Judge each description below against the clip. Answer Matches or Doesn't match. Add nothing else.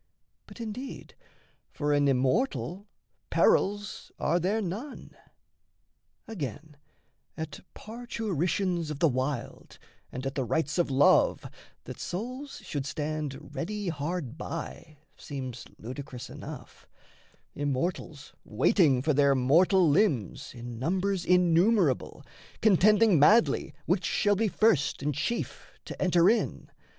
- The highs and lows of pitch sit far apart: Matches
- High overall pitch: Doesn't match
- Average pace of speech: Doesn't match